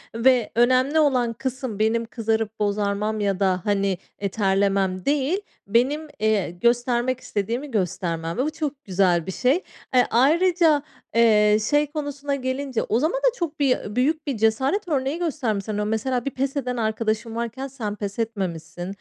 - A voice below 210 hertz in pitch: No, high, 235 Hz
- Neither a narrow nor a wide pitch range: Yes, average, 4.9 semitones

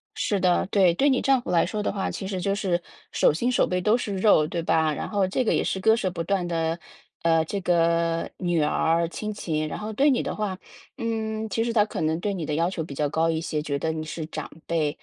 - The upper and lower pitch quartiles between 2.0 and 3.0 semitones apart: No, average, 4.4 semitones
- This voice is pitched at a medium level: Yes, medium, 180 Hz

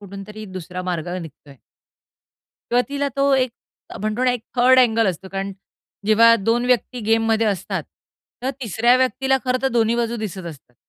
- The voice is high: Yes, high, 225 Hz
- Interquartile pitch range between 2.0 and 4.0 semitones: No, average, 4.4 semitones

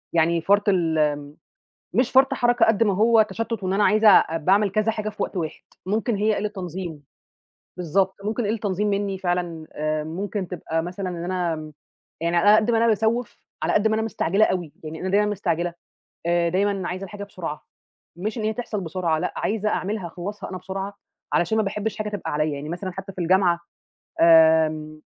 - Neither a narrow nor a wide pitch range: Yes, average, 3.8 semitones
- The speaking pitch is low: No, high, 190 Hz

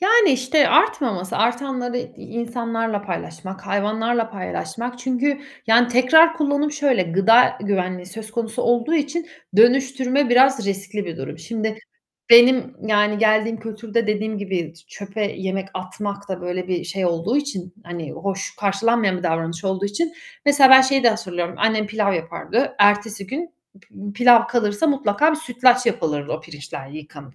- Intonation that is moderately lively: Yes, average, 4.7 semitones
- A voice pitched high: Yes, high, 220 Hz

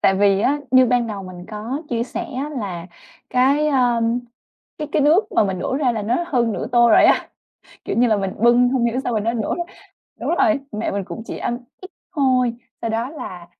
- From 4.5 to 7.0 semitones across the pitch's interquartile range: No, average, 3.7 semitones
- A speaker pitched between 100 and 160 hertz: No, high, 240 Hz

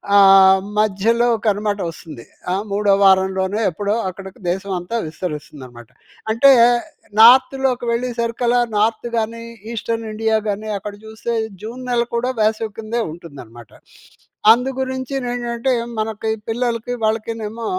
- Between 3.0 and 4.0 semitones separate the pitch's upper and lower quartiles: Yes, average, 3.4 semitones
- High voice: Yes, high, 220 Hz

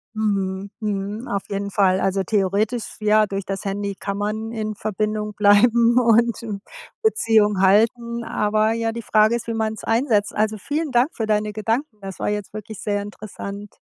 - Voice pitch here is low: No, high, 215 Hz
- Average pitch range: No, narrow, 1.9 semitones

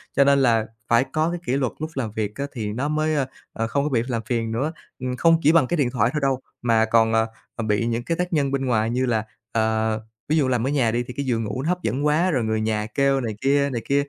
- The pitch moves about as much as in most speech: Yes, average, 4.0 semitones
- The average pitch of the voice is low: Yes, low, 125 Hz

